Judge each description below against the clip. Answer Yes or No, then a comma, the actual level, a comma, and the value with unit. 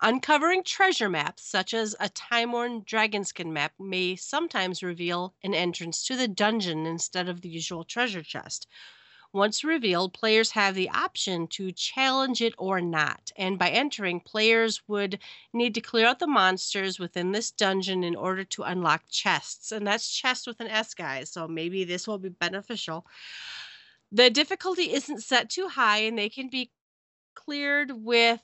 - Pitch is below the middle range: No, high, 205 Hz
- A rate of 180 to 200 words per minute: No, average, 165 wpm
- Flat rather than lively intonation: No, average, 4.8 semitones